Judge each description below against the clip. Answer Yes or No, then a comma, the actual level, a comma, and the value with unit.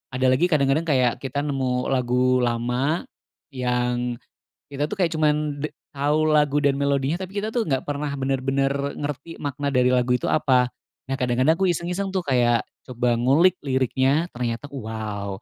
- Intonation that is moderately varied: Yes, average, 3.0 semitones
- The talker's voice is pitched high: No, low, 135 Hz